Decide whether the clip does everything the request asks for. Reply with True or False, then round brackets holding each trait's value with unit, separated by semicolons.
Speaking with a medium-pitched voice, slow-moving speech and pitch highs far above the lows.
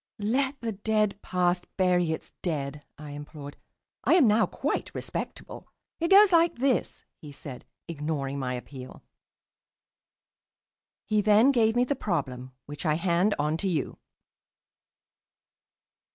True (180 Hz; 130 wpm; 7.0 semitones)